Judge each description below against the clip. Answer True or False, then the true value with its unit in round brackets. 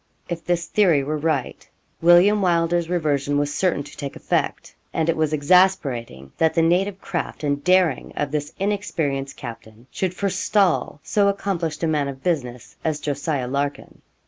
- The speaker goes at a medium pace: True (160 wpm)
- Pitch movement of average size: True (4.1 semitones)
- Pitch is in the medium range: True (160 Hz)